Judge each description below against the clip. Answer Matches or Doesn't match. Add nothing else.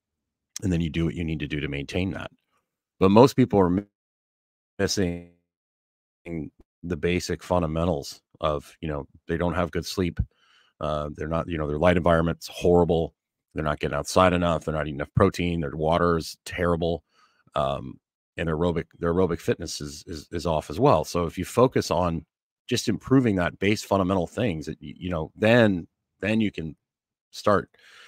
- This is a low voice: Matches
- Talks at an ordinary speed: Matches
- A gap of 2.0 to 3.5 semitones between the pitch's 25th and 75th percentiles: Matches